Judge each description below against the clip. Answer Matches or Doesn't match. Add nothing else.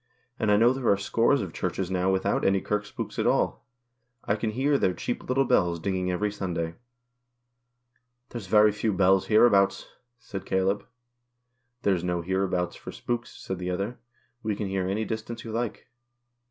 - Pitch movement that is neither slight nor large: Matches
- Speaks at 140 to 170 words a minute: Doesn't match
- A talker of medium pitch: Doesn't match